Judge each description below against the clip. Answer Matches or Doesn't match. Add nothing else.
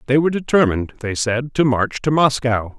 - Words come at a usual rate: Matches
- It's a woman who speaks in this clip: Doesn't match